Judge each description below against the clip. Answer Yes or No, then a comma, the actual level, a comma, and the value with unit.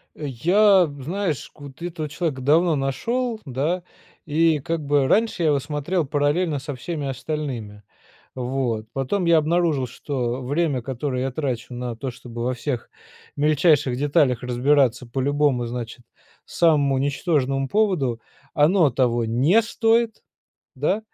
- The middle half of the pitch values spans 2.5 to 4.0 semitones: No, average, 4.4 semitones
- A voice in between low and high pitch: Yes, medium, 145 Hz